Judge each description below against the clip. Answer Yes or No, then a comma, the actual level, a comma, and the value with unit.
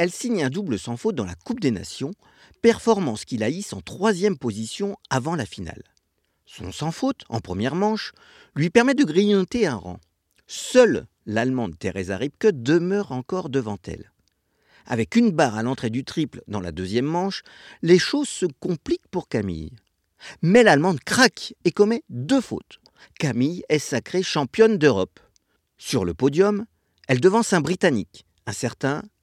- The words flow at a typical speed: Yes, average, 160 wpm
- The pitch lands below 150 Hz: No, medium, 160 Hz